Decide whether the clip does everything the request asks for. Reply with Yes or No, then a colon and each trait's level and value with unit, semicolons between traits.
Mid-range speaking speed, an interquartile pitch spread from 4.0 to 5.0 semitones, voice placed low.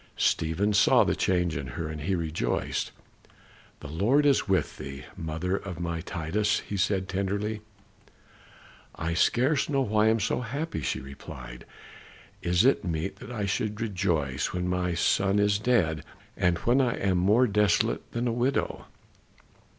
Yes: average, 160 wpm; average, 4.6 semitones; very low, 95 Hz